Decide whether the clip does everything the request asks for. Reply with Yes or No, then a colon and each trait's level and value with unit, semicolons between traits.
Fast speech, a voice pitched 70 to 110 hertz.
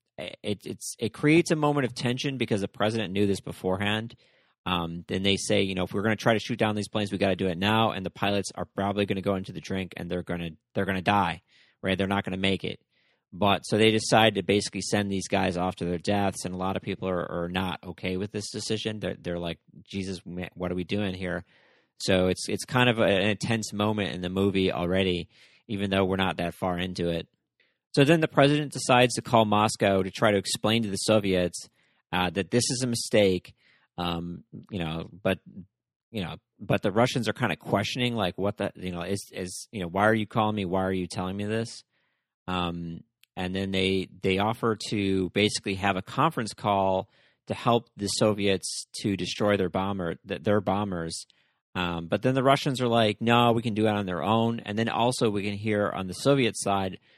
Yes: fast, 230 wpm; low, 100 Hz